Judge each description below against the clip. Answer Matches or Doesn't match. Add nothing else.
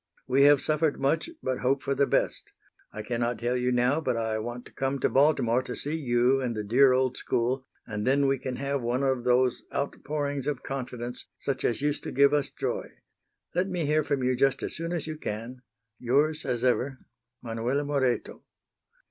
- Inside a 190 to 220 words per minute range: Matches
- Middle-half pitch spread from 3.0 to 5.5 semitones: Doesn't match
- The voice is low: Matches